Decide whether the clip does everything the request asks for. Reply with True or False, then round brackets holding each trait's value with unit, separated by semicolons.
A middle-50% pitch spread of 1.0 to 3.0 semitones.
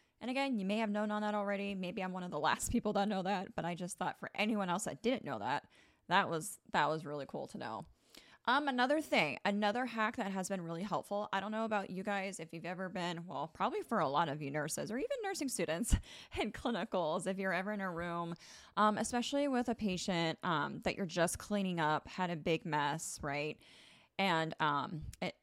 False (4.0 semitones)